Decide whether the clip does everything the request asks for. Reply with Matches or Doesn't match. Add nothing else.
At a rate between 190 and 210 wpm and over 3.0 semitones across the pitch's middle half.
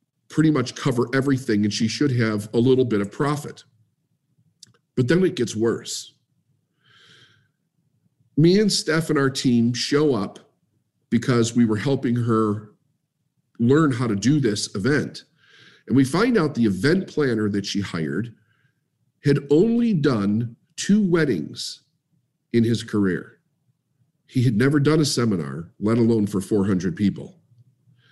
Doesn't match